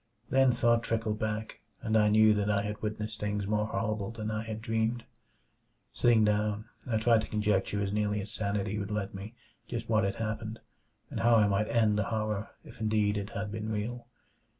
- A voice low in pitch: Yes, low, 110 Hz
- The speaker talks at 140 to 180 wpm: No, average, 195 wpm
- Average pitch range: No, narrow, 1.2 semitones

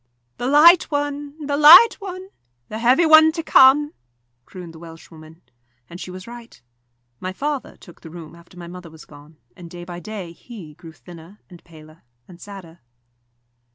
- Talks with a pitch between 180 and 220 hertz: Yes, medium, 185 Hz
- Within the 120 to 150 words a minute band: No, average, 170 wpm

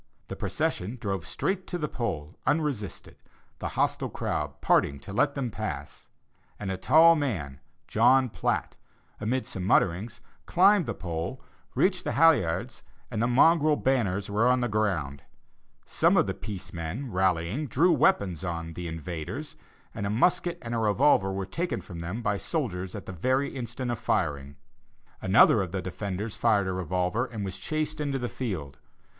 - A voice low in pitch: Yes, low, 105 Hz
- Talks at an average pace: Yes, average, 165 wpm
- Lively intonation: Yes, wide, 6.6 semitones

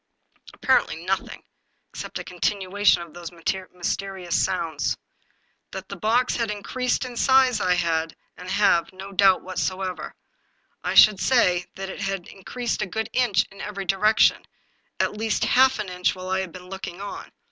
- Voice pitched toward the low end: No, high, 195 Hz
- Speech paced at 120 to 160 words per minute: No, average, 170 wpm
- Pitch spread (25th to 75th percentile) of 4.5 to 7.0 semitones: No, average, 2.7 semitones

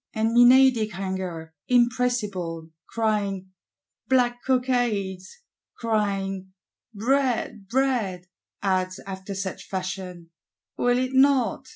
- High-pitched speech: Yes, high, 210 Hz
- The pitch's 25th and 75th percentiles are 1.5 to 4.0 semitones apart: No, average, 4.6 semitones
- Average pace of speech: No, slow, 85 wpm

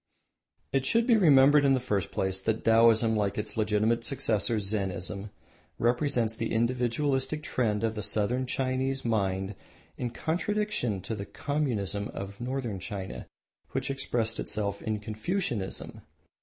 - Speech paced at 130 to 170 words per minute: Yes, average, 140 wpm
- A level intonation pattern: No, average, 4.2 semitones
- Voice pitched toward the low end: Yes, low, 115 Hz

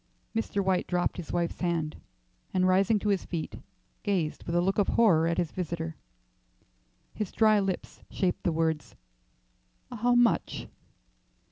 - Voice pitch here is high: No, medium, 180 Hz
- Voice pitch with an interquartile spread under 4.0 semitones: Yes, average, 3.3 semitones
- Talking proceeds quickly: No, average, 145 wpm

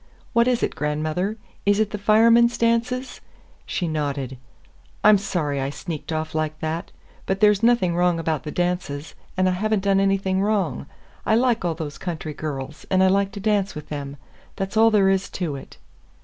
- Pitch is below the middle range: No, medium, 185 Hz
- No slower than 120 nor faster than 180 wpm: No, average, 190 wpm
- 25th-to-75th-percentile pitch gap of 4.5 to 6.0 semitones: Yes, average, 5.1 semitones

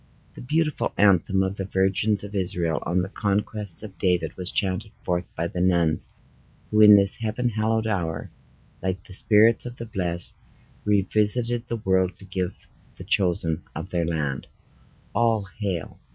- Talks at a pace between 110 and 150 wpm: No, average, 160 wpm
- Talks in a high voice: No, very low, 95 Hz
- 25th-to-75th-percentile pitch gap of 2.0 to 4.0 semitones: Yes, average, 3.2 semitones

